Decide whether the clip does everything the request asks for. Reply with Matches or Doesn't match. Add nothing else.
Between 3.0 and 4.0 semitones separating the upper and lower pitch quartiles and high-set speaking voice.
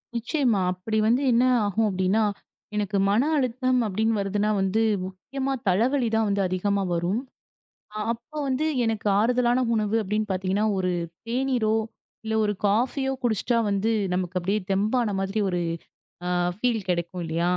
Matches